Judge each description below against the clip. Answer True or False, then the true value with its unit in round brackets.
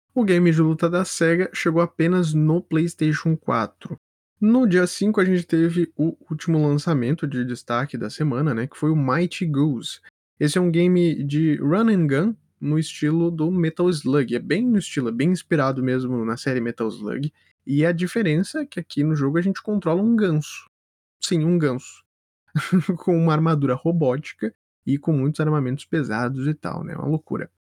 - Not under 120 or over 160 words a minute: False (185 wpm)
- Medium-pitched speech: True (160 Hz)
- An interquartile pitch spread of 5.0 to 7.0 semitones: False (3.6 semitones)